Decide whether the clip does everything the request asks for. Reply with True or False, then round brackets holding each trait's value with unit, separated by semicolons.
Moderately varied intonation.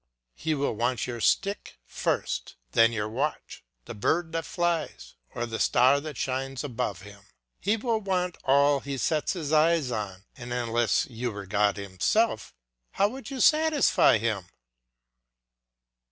False (6.8 semitones)